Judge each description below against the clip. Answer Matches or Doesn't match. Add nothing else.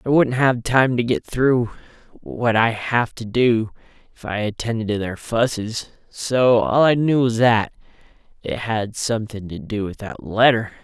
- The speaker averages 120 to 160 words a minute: Doesn't match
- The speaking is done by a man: Matches